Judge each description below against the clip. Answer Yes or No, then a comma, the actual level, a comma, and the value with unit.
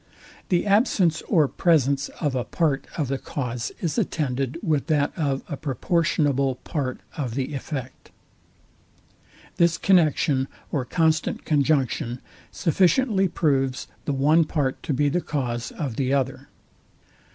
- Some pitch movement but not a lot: Yes, average, 3.6 semitones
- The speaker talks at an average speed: No, slow, 130 wpm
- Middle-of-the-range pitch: Yes, medium, 145 Hz